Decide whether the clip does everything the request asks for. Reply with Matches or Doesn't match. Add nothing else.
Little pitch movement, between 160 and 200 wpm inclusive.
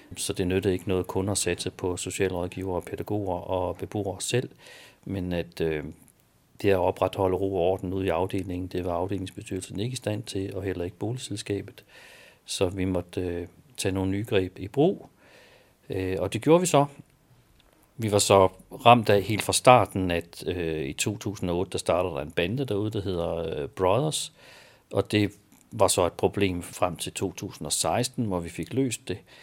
Matches